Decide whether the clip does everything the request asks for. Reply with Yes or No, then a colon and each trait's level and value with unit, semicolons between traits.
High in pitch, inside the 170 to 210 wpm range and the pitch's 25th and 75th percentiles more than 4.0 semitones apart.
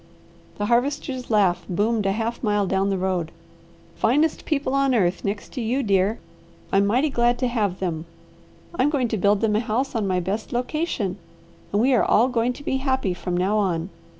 Yes: high, 220 Hz; average, 195 wpm; average, 4.6 semitones